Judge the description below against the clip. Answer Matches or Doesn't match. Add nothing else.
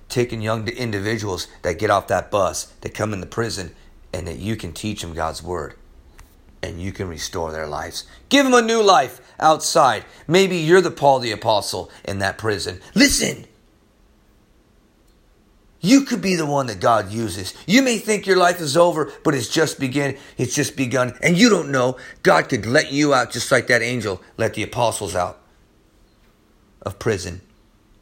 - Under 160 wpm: Doesn't match